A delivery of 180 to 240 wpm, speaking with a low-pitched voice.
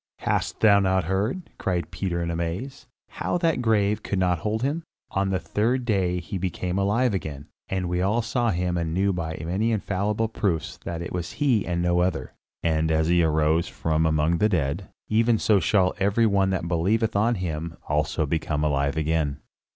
Yes: average, 190 wpm; very low, 90 Hz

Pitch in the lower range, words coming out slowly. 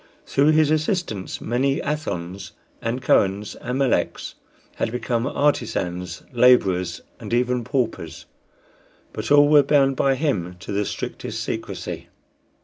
Yes: low, 125 Hz; slow, 125 wpm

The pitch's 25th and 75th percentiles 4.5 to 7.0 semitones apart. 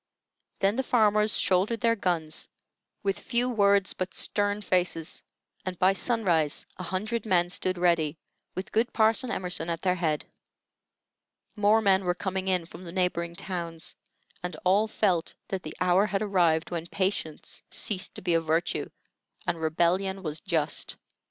No: average, 3.1 semitones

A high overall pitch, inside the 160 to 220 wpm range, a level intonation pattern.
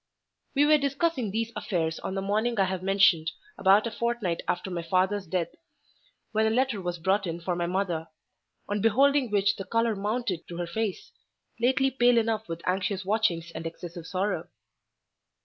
No: high, 195 Hz; average, 170 wpm; average, 4.4 semitones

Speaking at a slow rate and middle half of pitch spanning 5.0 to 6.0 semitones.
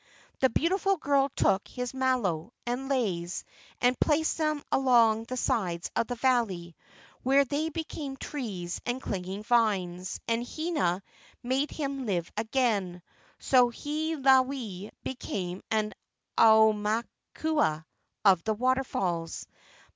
Yes: slow, 115 wpm; wide, 5.6 semitones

